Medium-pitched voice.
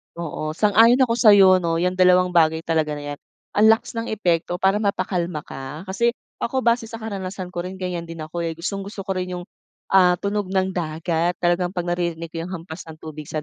Yes: medium, 180 Hz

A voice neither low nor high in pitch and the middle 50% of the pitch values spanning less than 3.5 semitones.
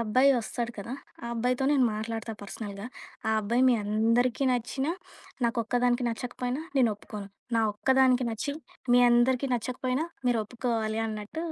No: high, 240 Hz; narrow, 2.4 semitones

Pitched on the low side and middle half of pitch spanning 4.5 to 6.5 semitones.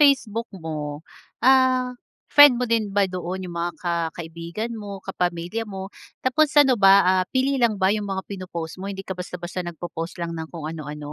No: medium, 185 Hz; average, 5.2 semitones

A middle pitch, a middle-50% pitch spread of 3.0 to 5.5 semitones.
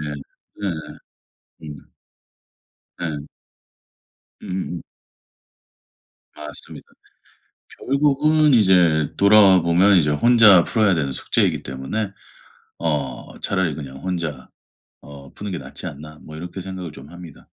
No: very low, 85 Hz; average, 5.1 semitones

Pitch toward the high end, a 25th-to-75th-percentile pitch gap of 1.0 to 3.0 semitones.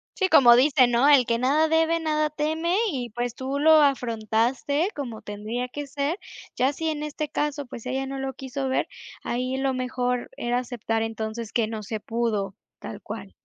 No: very high, 260 Hz; average, 3.7 semitones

